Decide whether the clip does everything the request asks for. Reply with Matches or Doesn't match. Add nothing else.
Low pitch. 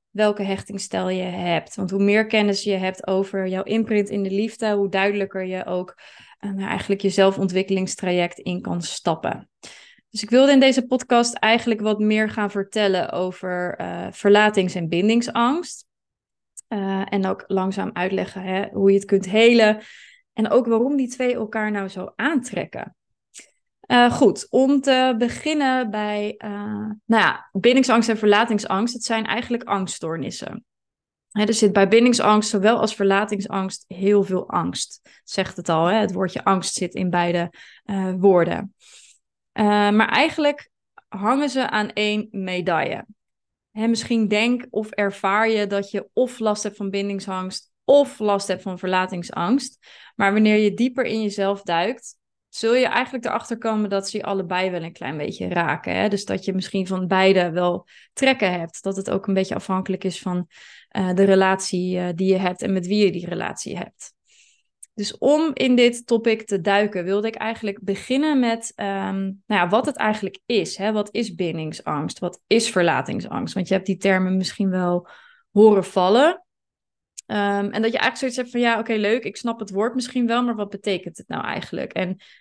Doesn't match